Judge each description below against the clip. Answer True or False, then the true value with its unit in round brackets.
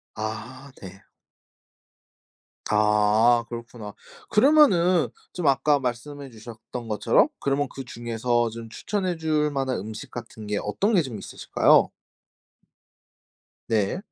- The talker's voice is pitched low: True (120 Hz)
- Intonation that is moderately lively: True (4.8 semitones)